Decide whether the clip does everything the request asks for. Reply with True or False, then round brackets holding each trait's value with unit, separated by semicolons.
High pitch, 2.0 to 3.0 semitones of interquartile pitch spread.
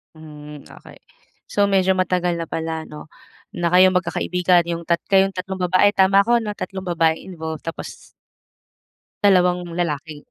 False (180 Hz; 2.6 semitones)